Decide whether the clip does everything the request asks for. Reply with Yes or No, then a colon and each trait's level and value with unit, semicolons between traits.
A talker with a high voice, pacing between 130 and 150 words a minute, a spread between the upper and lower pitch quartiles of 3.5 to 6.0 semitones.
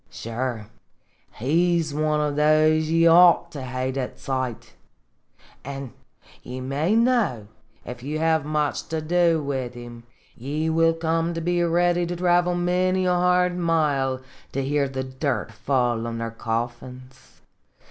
No: medium, 150 Hz; average, 145 wpm; average, 4.7 semitones